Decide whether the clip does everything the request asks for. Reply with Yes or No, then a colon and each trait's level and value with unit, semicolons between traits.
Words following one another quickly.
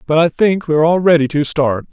Yes: fast, 250 wpm